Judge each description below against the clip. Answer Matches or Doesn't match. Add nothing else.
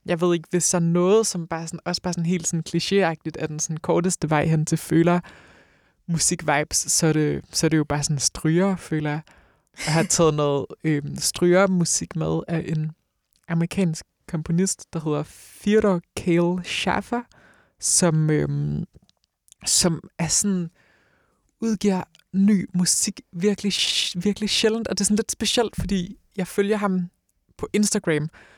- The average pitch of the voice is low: Doesn't match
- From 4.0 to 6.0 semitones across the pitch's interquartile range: Doesn't match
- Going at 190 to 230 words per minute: Doesn't match